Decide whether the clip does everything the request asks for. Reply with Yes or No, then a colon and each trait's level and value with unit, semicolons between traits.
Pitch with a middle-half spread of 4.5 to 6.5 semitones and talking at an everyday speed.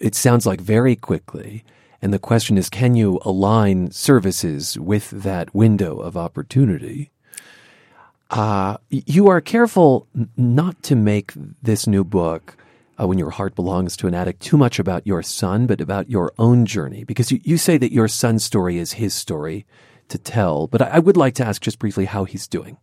Yes: average, 5.3 semitones; average, 185 wpm